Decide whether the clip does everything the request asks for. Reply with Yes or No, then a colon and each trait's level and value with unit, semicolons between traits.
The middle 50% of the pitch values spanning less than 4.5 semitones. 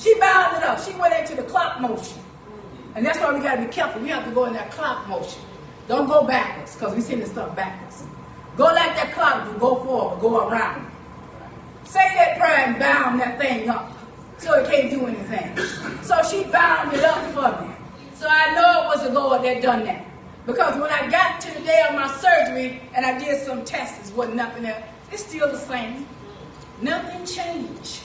No: average, 5.3 semitones